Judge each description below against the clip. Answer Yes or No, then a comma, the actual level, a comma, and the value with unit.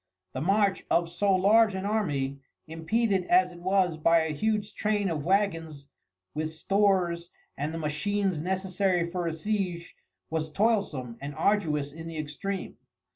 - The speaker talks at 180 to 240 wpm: No, average, 150 wpm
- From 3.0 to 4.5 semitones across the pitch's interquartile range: Yes, average, 4.0 semitones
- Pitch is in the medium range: Yes, medium, 175 Hz